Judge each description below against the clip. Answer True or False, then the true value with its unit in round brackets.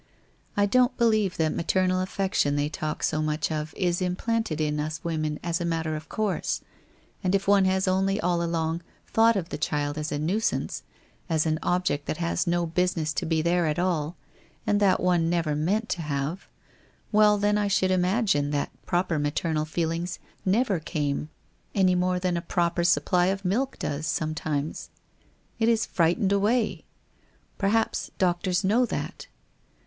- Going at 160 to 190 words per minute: True (170 wpm)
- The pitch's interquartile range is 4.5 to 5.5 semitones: False (3.8 semitones)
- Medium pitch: True (175 Hz)